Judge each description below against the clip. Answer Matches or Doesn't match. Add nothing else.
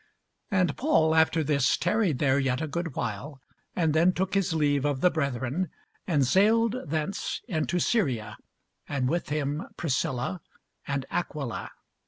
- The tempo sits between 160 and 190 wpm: Doesn't match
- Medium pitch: Matches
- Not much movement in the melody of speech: Doesn't match